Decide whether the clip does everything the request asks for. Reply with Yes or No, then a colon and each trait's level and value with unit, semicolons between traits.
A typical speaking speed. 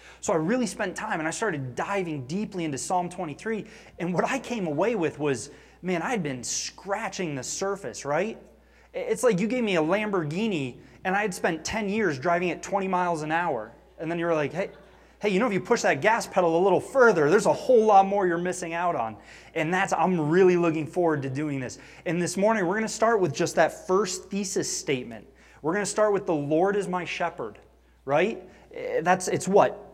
No: fast, 215 wpm